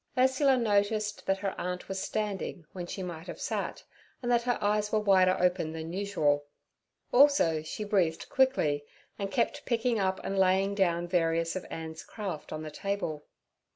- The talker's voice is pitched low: No, high, 190 Hz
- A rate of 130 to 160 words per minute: No, average, 170 wpm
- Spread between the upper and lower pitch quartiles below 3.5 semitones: No, average, 4.1 semitones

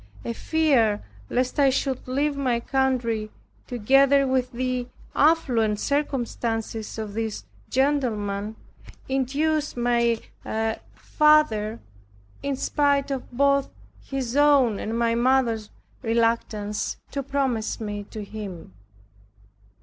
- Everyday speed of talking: No, slow, 105 wpm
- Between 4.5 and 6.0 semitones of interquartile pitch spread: No, average, 3.7 semitones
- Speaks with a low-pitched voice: No, very high, 250 Hz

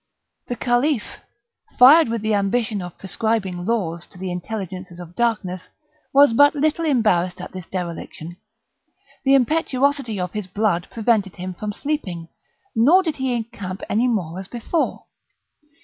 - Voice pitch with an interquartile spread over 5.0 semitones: Yes, wide, 5.4 semitones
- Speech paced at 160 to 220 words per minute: No, average, 145 wpm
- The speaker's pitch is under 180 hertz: No, high, 215 Hz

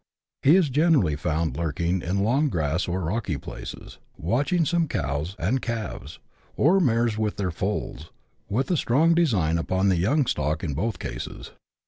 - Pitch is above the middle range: No, low, 100 Hz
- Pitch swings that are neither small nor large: No, wide, 8.5 semitones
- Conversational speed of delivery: Yes, average, 165 wpm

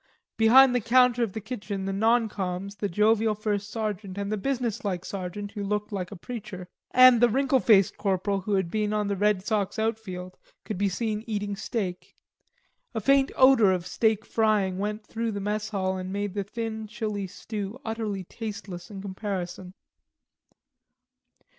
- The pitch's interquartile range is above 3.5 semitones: No, narrow, 2.4 semitones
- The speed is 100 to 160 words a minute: No, average, 170 wpm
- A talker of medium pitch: No, high, 210 Hz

